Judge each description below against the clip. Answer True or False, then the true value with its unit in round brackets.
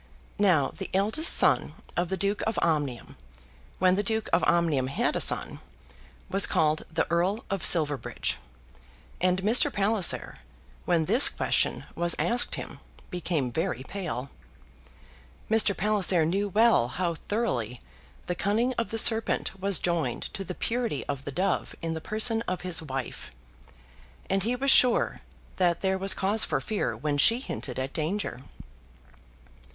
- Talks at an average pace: True (150 wpm)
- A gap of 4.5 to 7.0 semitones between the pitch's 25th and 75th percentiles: True (4.8 semitones)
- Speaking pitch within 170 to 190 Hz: True (185 Hz)